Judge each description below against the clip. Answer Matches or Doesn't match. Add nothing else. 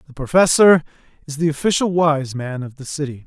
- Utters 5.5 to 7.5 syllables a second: Matches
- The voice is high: Doesn't match